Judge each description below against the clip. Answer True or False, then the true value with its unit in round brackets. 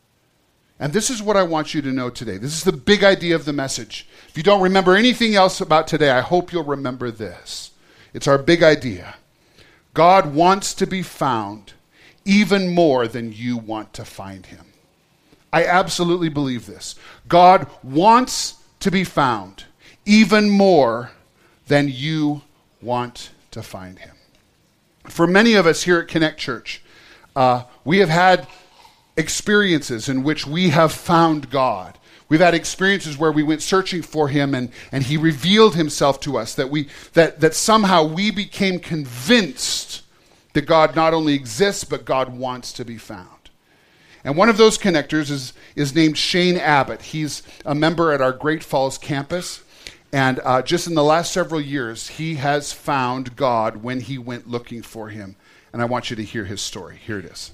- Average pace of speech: True (175 wpm)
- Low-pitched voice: False (155 Hz)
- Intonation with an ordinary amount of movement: False (5.8 semitones)